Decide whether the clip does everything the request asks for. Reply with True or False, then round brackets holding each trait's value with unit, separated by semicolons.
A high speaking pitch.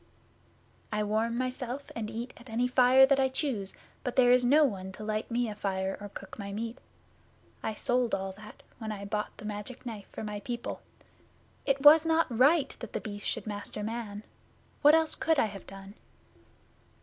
True (230 Hz)